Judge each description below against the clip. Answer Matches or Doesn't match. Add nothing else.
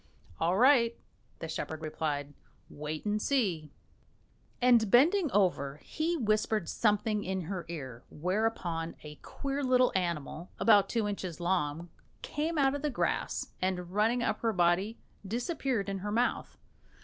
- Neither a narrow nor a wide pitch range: Doesn't match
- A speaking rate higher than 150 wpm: Doesn't match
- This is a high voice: Matches